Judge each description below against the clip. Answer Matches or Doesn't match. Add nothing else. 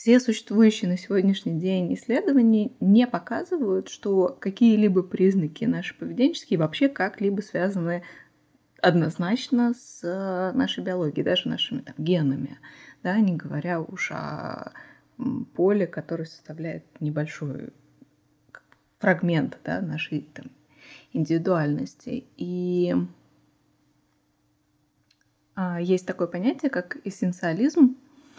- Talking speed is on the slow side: Matches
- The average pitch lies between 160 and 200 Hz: Matches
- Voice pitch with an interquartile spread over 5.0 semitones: Matches